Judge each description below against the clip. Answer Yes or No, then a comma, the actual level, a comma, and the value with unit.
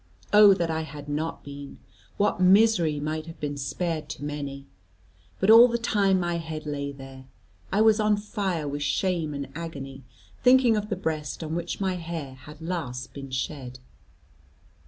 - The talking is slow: No, average, 170 wpm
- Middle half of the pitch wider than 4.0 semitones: Yes, average, 5.0 semitones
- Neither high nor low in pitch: Yes, medium, 160 Hz